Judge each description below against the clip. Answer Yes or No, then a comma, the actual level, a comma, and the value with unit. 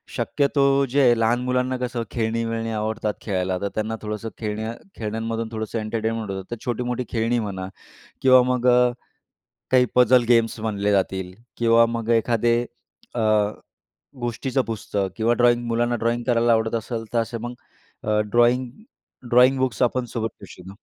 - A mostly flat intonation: Yes, narrow, 1.9 semitones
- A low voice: Yes, low, 115 Hz